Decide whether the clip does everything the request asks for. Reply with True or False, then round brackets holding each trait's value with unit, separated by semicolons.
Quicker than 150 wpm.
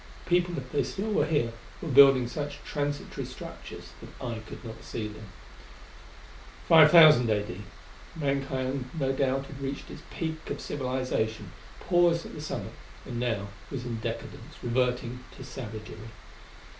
False (145 wpm)